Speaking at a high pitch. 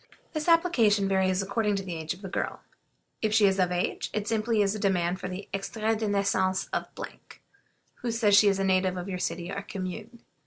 Yes: high, 195 Hz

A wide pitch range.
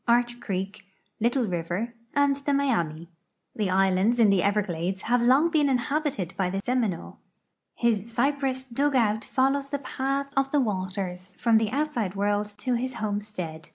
Yes: wide, 5.7 semitones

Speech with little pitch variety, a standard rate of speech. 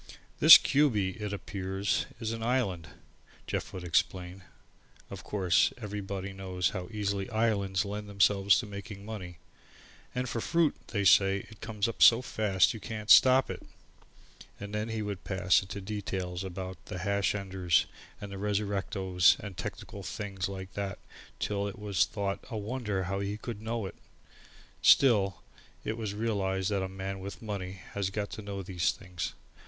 Yes: narrow, 1.9 semitones; average, 165 wpm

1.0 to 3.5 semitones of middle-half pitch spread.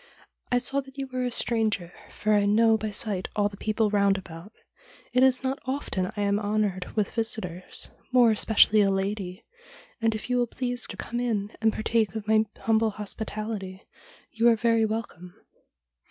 Yes: narrow, 2.5 semitones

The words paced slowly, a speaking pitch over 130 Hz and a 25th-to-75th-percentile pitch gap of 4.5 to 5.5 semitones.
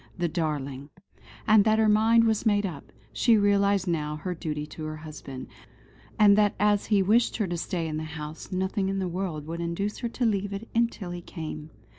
No: fast, 205 wpm; medium, 185 Hz; average, 4.8 semitones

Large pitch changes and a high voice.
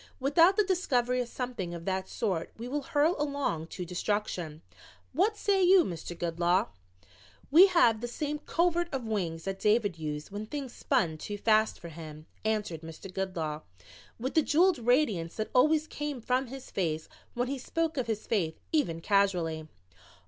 Yes: wide, 8.9 semitones; high, 220 Hz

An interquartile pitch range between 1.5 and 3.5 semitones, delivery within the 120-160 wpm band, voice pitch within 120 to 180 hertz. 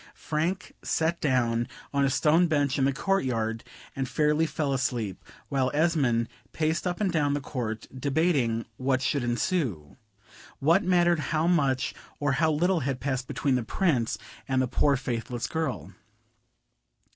No: average, 4.2 semitones; average, 155 wpm; medium, 140 Hz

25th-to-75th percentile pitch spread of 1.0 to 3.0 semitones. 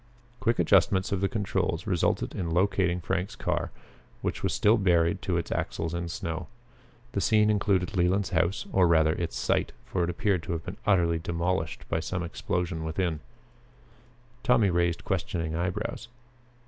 Yes: narrow, 2.6 semitones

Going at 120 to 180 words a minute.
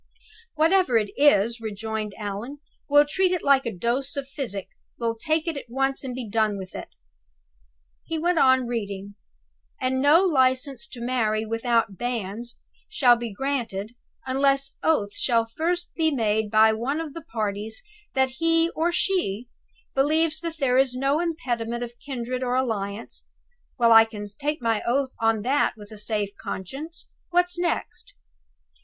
Yes: average, 160 wpm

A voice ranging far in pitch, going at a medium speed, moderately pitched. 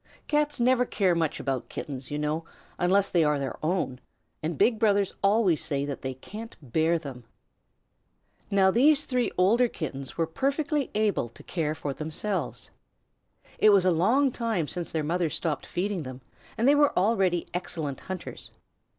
Yes: wide, 6.5 semitones; average, 165 wpm; medium, 180 Hz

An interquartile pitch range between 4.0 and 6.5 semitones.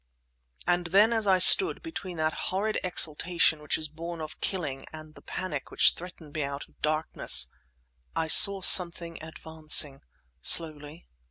No: average, 3.0 semitones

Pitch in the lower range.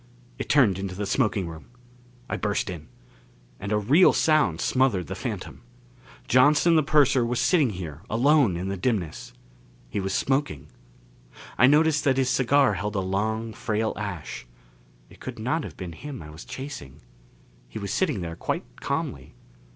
Yes: low, 110 Hz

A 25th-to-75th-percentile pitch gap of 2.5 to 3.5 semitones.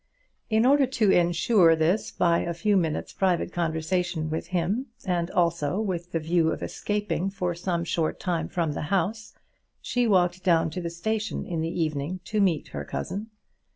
Yes: average, 3.1 semitones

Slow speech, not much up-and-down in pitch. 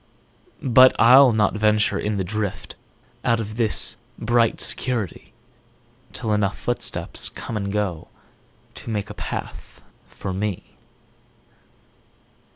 Yes: slow, 100 wpm; narrow, 2.2 semitones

